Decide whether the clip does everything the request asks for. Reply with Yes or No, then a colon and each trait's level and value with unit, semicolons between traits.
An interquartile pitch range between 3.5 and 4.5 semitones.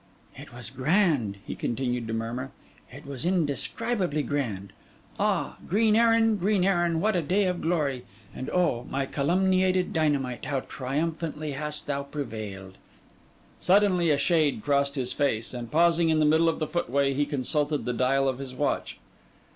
No: average, 5.1 semitones